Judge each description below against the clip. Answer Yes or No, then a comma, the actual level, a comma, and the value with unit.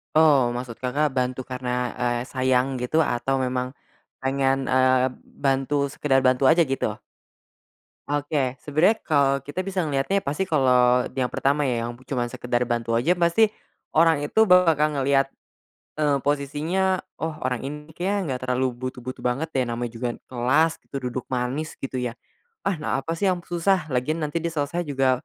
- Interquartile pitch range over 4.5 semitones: No, average, 3.5 semitones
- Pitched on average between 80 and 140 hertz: Yes, low, 135 Hz